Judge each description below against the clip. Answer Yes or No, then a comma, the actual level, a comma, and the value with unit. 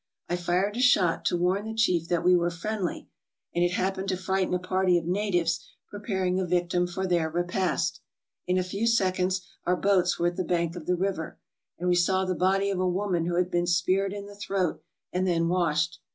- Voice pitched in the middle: Yes, medium, 180 Hz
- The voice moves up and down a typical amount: No, narrow, 1.6 semitones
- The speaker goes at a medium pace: No, fast, 215 wpm